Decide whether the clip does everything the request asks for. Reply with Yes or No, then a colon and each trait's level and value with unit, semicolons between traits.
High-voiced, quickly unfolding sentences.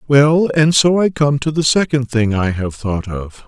No: low, 135 Hz; fast, 225 wpm